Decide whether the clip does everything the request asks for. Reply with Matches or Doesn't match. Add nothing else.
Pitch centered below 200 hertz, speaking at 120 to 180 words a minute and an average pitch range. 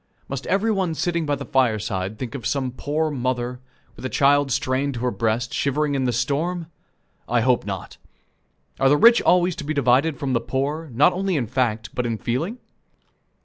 Doesn't match